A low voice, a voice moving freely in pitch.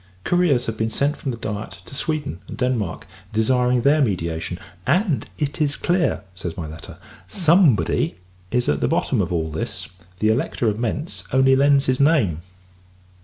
Yes: low, 125 Hz; wide, 6.3 semitones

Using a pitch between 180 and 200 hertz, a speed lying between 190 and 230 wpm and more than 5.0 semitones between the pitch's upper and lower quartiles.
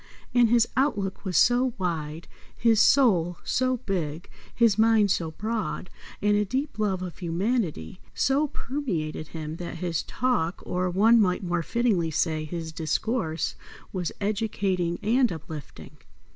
No: high, 190 Hz; average, 140 wpm; wide, 5.6 semitones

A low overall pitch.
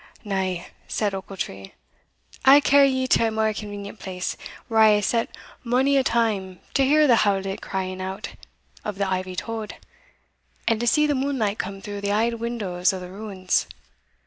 No: high, 210 Hz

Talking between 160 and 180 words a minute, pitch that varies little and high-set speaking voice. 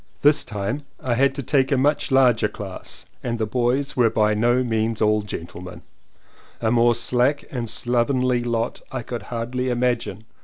No: average, 175 wpm; narrow, 2.2 semitones; low, 120 Hz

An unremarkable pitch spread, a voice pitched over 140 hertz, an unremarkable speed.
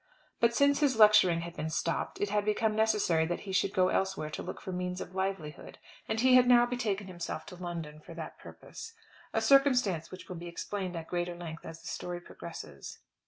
No: average, 4.3 semitones; medium, 185 Hz; fast, 210 wpm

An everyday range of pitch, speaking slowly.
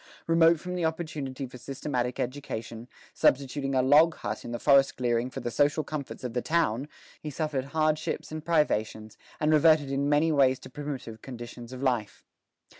No: average, 3.8 semitones; average, 175 wpm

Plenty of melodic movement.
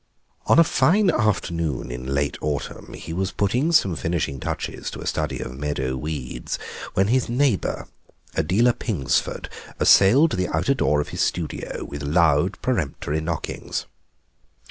Yes: wide, 7.1 semitones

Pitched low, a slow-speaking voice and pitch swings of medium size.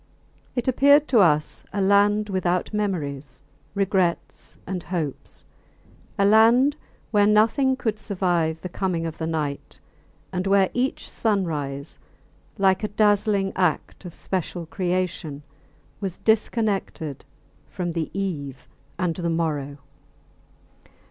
No: medium, 185 Hz; slow, 115 wpm; average, 4.2 semitones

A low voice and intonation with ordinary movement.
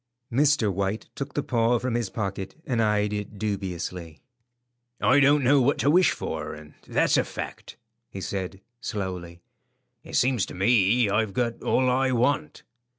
Yes: low, 110 Hz; average, 4.8 semitones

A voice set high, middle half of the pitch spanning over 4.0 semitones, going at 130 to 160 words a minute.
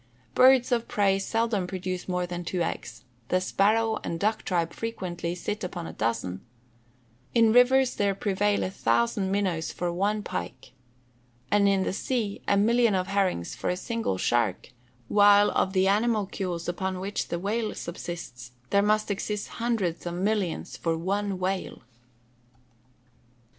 No: high, 195 Hz; average, 3.2 semitones; average, 150 wpm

